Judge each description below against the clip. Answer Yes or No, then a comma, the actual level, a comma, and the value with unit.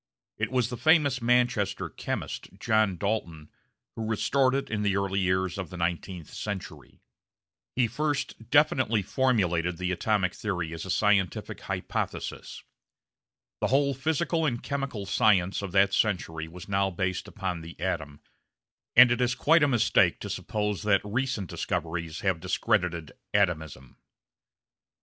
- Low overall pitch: Yes, low, 100 Hz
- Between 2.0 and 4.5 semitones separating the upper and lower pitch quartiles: No, wide, 5.4 semitones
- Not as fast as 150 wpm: Yes, average, 140 wpm